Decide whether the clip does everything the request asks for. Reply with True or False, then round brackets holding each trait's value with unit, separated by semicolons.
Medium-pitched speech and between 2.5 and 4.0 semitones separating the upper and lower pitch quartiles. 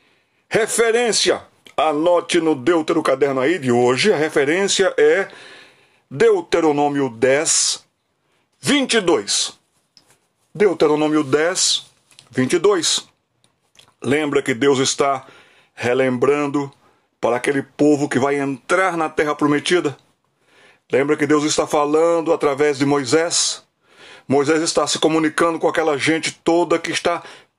True (155 Hz; 3.4 semitones)